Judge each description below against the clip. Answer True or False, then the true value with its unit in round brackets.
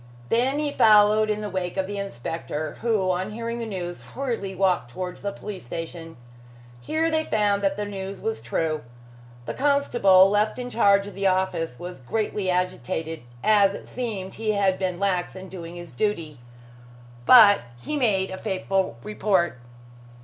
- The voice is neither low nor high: False (195 Hz)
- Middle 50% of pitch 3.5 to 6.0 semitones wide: False (3.1 semitones)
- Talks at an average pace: True (165 wpm)